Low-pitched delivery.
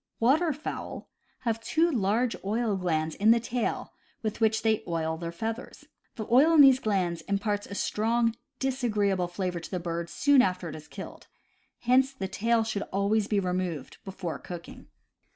No: high, 210 Hz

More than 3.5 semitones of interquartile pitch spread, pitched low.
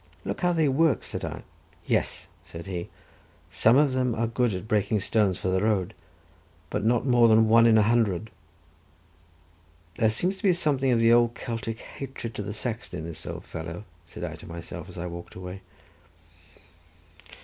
Yes: average, 4.6 semitones; low, 110 Hz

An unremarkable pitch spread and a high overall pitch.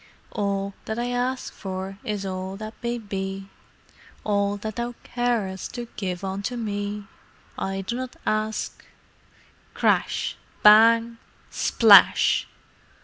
Yes: average, 3.3 semitones; high, 210 Hz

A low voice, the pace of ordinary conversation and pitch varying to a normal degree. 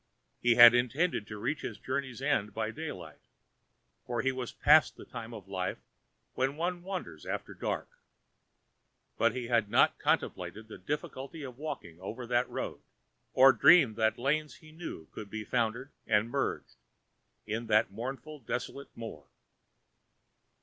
Yes: low, 120 Hz; average, 150 wpm; average, 4.2 semitones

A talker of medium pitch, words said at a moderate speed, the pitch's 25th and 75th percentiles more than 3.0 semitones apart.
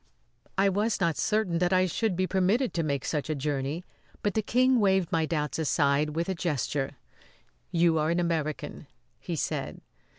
Yes: medium, 170 Hz; average, 175 wpm; average, 3.9 semitones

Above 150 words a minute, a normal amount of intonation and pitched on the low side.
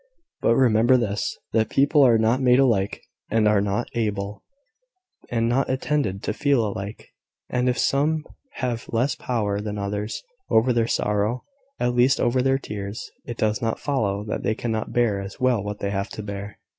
Yes: average, 180 wpm; average, 3.5 semitones; low, 115 Hz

